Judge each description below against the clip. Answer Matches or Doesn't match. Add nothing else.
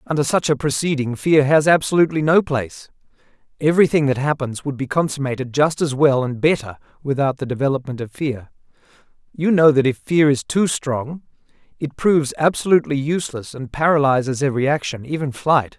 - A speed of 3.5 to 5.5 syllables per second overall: Doesn't match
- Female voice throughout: Doesn't match